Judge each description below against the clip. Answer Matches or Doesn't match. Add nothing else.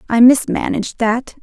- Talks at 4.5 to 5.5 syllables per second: Matches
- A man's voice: Doesn't match